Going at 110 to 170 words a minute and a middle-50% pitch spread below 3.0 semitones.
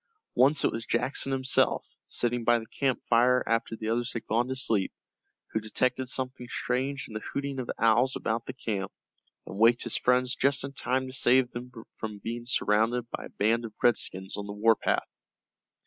No: average, 195 wpm; narrow, 2.4 semitones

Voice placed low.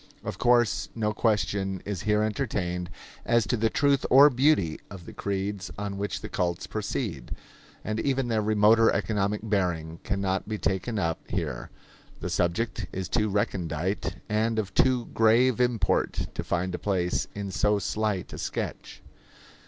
Yes: low, 105 Hz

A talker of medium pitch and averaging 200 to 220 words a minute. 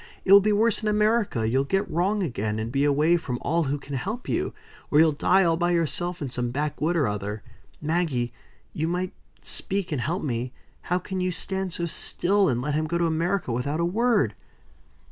Yes: medium, 165 Hz; fast, 205 wpm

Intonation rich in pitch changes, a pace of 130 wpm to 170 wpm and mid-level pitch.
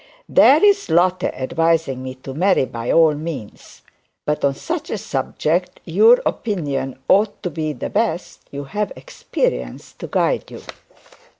Yes: wide, 6.9 semitones; average, 140 wpm; medium, 160 Hz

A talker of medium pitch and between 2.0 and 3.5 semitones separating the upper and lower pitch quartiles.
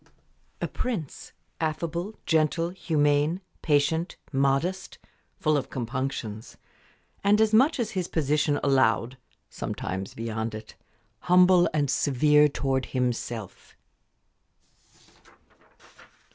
No: medium, 150 Hz; average, 4.8 semitones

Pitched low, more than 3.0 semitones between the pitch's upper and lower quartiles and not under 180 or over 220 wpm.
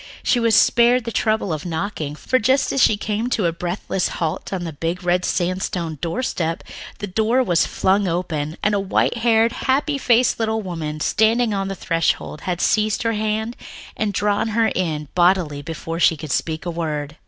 No: high, 190 Hz; average, 5.0 semitones; average, 185 wpm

